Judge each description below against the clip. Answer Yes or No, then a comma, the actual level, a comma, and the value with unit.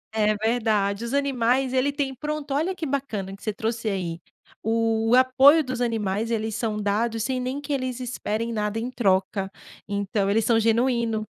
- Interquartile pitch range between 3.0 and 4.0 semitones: Yes, average, 3.4 semitones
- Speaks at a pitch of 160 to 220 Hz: No, high, 230 Hz